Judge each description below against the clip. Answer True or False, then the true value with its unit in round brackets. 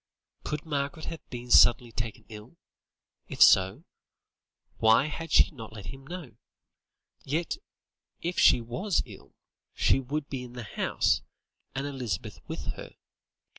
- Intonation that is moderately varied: True (4.6 semitones)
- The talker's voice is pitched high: False (135 Hz)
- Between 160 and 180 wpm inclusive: False (135 wpm)